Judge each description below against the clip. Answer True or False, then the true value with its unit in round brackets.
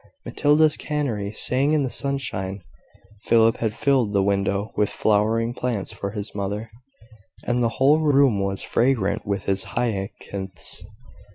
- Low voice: True (110 Hz)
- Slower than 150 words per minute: True (140 wpm)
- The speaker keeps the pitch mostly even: False (4.9 semitones)